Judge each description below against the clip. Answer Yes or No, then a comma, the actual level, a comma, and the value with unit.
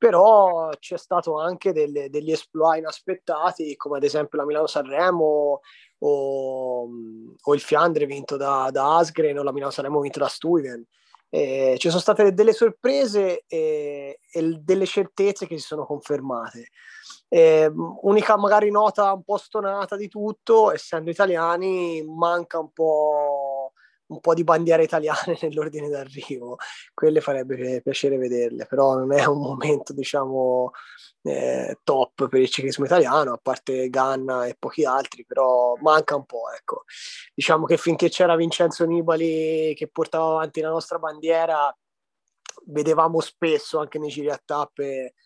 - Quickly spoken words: No, average, 145 wpm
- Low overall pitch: No, medium, 155 Hz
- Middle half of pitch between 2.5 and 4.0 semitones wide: Yes, average, 3.7 semitones